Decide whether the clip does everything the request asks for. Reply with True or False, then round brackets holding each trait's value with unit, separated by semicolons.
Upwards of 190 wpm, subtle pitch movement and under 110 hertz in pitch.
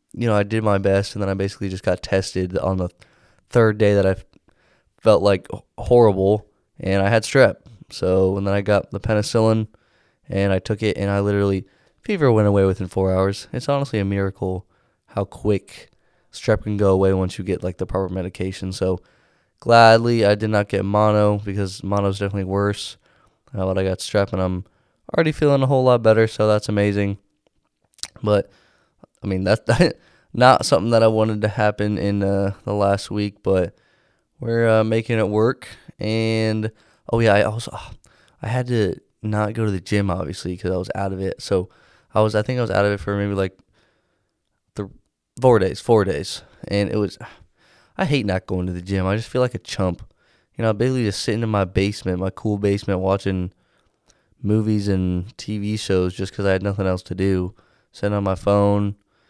True (200 wpm; 2.3 semitones; 100 Hz)